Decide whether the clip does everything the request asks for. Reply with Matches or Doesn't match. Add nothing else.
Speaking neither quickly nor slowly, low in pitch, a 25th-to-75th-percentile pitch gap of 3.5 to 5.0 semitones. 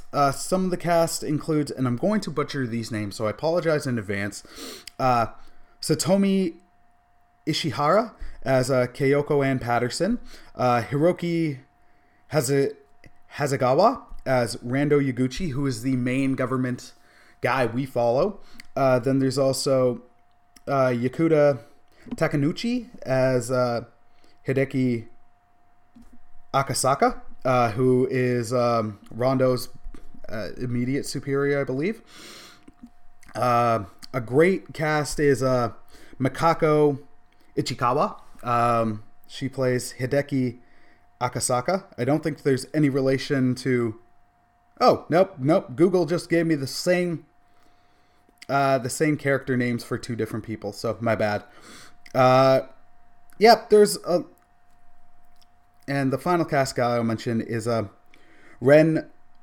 Doesn't match